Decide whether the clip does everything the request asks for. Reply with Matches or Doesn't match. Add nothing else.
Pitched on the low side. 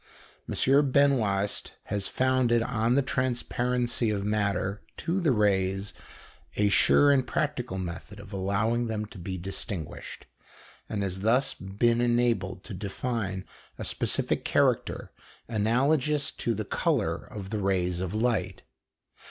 Matches